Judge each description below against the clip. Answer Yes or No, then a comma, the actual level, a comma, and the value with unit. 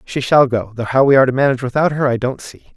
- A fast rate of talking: Yes, fast, 305 wpm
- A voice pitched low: Yes, low, 130 Hz